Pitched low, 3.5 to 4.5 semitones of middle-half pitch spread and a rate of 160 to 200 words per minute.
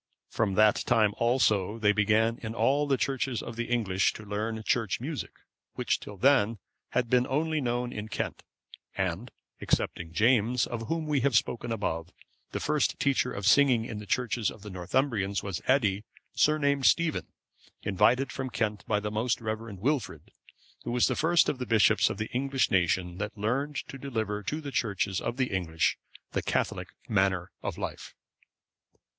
Yes: low, 115 Hz; average, 4.1 semitones; average, 175 wpm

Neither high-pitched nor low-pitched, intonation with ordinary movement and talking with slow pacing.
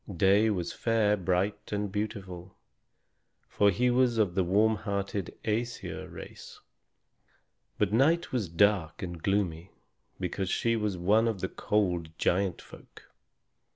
No: low, 100 Hz; average, 3.0 semitones; slow, 130 wpm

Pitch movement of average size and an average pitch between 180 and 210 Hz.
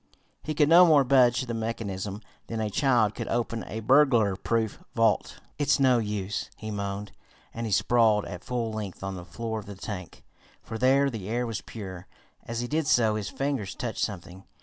No: average, 3.3 semitones; low, 110 Hz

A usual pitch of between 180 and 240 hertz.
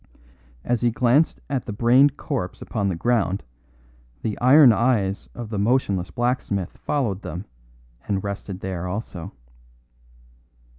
No: low, 110 Hz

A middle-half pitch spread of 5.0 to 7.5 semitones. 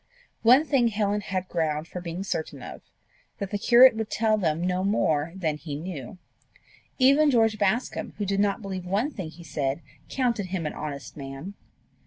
Yes: wide, 5.5 semitones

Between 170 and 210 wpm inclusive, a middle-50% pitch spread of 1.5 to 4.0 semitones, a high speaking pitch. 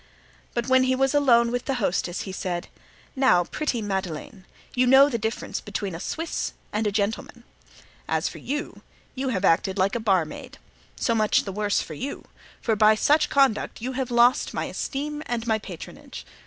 No: average, 180 wpm; average, 4.7 semitones; high, 230 Hz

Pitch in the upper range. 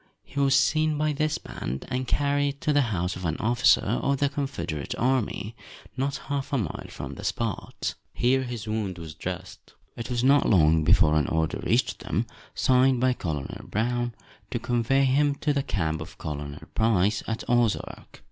No: low, 120 Hz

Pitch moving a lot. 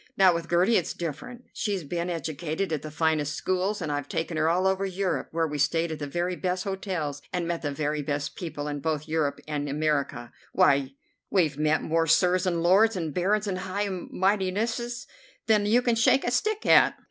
No: average, 4.0 semitones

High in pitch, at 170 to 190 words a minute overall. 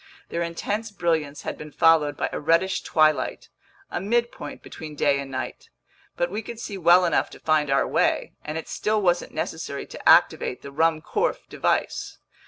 No: medium, 165 Hz; average, 175 wpm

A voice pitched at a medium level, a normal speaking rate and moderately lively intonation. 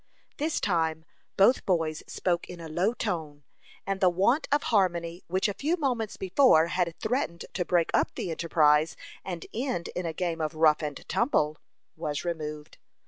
Yes: medium, 175 Hz; average, 170 wpm; average, 3.6 semitones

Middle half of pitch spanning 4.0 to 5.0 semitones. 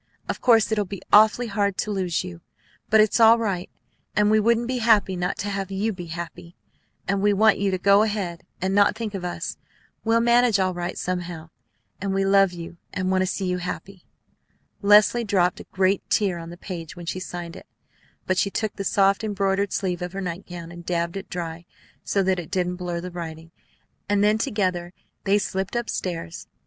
No: average, 2.7 semitones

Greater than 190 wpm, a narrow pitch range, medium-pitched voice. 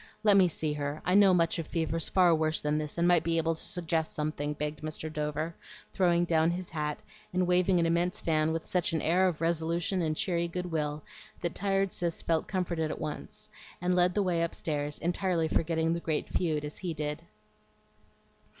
Yes: average, 200 wpm; narrow, 2.3 semitones; medium, 165 Hz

